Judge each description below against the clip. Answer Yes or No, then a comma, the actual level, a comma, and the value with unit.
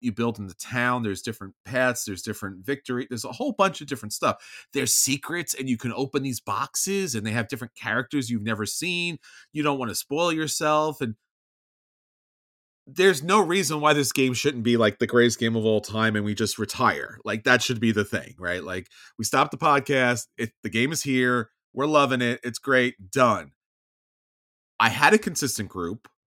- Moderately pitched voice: No, low, 125 Hz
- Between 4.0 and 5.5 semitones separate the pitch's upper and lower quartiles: Yes, average, 4.3 semitones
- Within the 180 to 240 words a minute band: Yes, average, 200 wpm